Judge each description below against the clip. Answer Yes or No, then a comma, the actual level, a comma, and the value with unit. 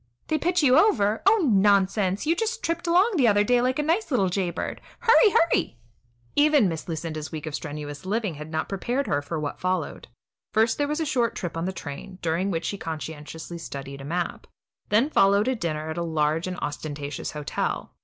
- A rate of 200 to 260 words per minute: Yes, fast, 205 wpm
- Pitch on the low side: No, high, 190 Hz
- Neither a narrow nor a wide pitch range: No, wide, 8.7 semitones